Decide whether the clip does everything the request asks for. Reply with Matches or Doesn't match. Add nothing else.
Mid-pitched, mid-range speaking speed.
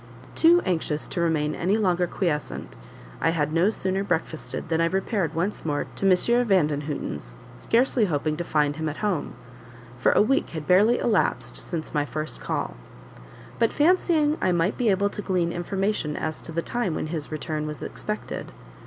Matches